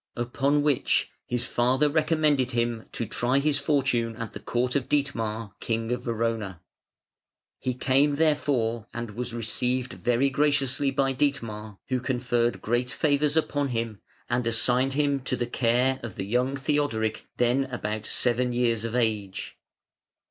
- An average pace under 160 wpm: Yes, average, 150 wpm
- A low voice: Yes, low, 125 Hz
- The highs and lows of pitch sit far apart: No, average, 3.1 semitones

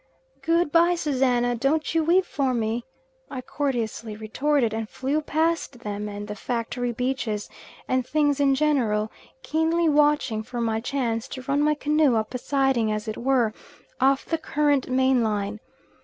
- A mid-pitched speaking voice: No, very high, 260 Hz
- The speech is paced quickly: No, average, 160 wpm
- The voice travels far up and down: No, average, 4.7 semitones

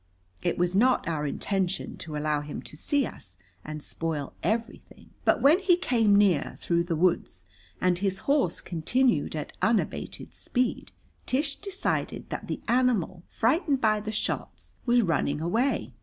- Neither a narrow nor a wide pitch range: No, wide, 7.5 semitones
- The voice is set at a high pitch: Yes, high, 195 Hz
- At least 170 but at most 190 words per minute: No, average, 155 wpm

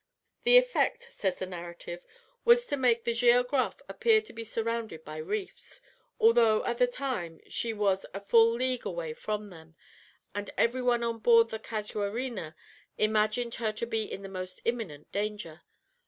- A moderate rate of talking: Yes, average, 165 wpm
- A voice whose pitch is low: No, high, 225 Hz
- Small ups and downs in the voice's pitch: No, average, 3.9 semitones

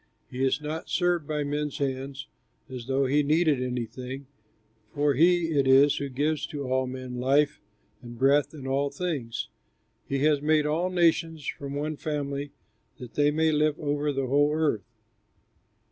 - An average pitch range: No, narrow, 2.3 semitones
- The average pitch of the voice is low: No, medium, 145 Hz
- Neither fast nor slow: Yes, average, 160 wpm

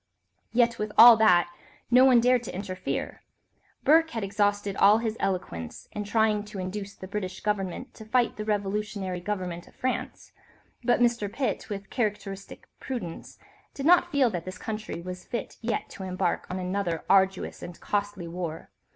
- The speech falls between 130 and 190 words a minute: Yes, average, 165 wpm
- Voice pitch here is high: Yes, high, 205 Hz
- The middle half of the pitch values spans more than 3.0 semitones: Yes, average, 3.6 semitones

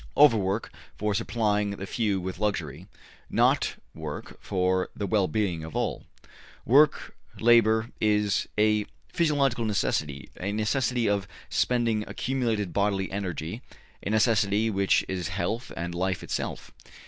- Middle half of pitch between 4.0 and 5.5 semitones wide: No, average, 3.2 semitones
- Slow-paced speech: Yes, slow, 125 wpm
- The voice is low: Yes, low, 105 Hz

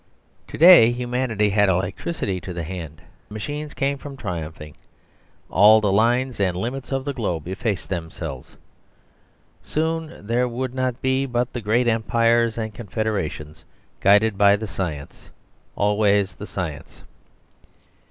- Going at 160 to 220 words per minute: No, slow, 135 wpm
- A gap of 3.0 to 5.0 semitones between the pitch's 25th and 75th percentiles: Yes, average, 4.7 semitones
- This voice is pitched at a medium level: No, low, 110 Hz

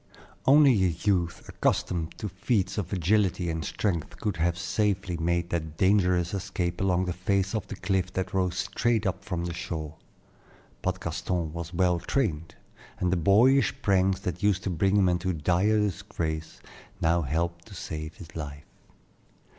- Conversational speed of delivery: Yes, average, 160 wpm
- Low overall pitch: Yes, very low, 90 Hz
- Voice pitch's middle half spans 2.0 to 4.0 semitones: Yes, narrow, 2.6 semitones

